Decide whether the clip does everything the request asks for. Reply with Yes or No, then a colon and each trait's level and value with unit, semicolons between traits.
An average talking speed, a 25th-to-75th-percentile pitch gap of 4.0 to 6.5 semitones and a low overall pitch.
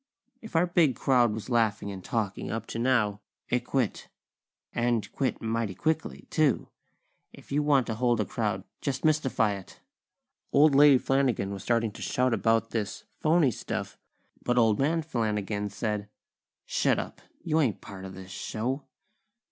Yes: average, 160 wpm; average, 4.6 semitones; low, 120 Hz